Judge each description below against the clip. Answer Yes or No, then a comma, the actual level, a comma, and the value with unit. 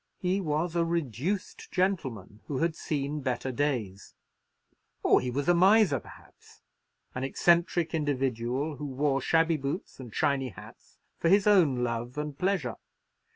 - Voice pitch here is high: No, medium, 145 Hz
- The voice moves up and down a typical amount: Yes, average, 4.9 semitones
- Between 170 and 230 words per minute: No, average, 140 wpm